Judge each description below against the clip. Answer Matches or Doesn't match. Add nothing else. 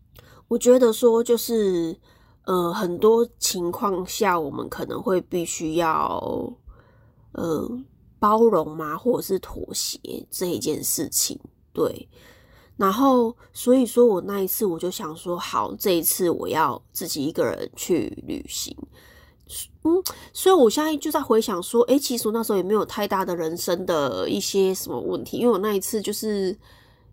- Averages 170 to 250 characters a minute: Matches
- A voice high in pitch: Matches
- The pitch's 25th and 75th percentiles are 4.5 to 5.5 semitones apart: Matches